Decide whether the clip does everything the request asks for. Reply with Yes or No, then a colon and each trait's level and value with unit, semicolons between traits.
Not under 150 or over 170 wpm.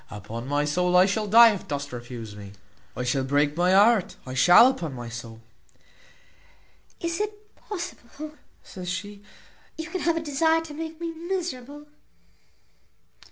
Yes: average, 160 wpm